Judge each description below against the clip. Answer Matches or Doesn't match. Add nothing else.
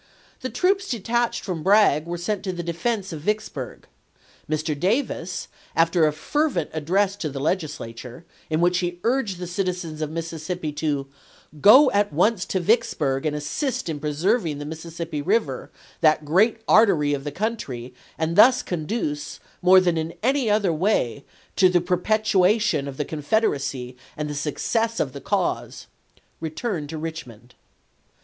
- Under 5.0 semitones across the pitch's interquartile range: Doesn't match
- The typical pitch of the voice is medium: Matches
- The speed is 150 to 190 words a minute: Matches